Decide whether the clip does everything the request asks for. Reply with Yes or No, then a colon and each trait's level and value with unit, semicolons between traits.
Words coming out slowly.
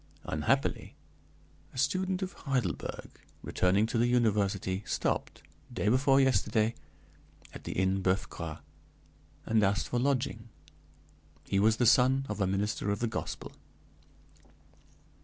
Yes: slow, 125 wpm